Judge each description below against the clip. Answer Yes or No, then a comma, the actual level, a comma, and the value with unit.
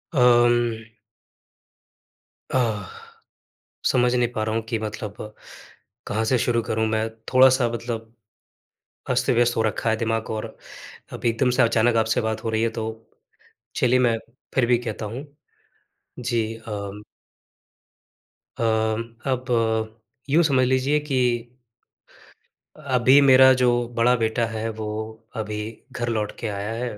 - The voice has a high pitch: No, low, 115 Hz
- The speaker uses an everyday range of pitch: No, narrow, 2.0 semitones